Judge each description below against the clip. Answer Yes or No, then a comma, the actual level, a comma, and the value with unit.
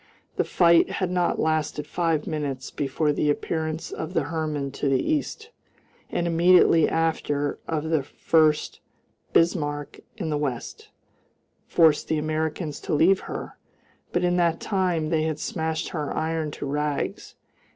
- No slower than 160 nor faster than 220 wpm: No, average, 145 wpm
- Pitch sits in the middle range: Yes, medium, 160 Hz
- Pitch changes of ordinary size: No, narrow, 2.2 semitones